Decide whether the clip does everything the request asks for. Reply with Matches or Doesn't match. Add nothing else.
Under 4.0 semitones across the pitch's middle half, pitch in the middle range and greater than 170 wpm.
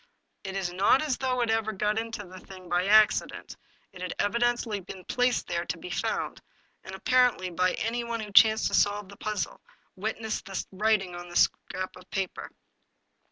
Doesn't match